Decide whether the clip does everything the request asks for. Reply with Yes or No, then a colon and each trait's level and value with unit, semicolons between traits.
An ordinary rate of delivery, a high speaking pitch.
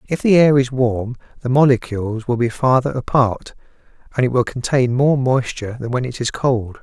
No: average, 195 wpm; low, 125 Hz